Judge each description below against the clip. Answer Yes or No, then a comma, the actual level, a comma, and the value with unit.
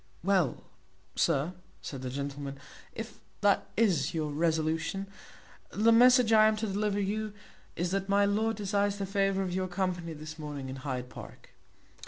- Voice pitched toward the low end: No, high, 190 Hz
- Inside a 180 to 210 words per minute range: No, average, 165 wpm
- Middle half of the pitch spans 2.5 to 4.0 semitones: No, average, 4.9 semitones